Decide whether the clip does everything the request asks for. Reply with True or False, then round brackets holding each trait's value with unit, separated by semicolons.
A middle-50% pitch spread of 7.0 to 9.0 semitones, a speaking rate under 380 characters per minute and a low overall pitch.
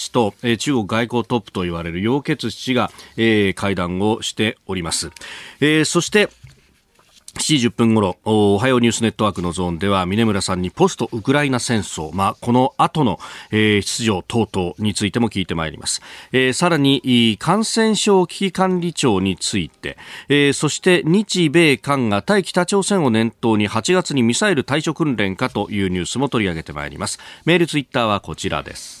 False (6.4 semitones; 335 characters per minute; 115 Hz)